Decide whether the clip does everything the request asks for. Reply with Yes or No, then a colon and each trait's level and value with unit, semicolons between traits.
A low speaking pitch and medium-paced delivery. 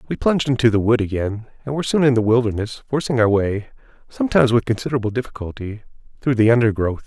Yes: low, 115 Hz; average, 185 wpm